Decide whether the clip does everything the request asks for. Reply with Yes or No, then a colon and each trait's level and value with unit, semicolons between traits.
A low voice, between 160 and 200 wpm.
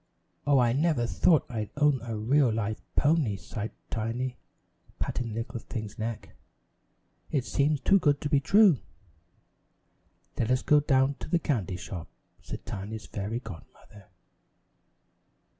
No: low, 125 Hz; average, 140 wpm